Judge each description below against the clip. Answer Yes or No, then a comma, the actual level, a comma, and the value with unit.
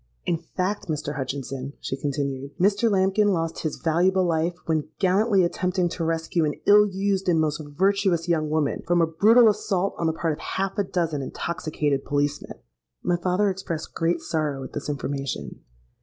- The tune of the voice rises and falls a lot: No, average, 4.1 semitones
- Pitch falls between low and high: Yes, medium, 165 Hz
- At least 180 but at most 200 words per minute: No, average, 170 wpm